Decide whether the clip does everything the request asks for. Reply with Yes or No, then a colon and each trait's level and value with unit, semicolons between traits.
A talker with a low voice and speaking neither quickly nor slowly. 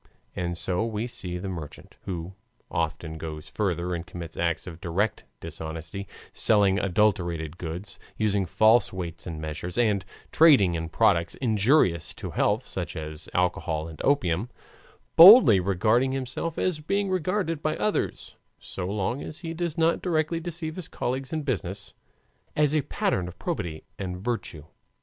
Yes: low, 100 Hz; average, 150 wpm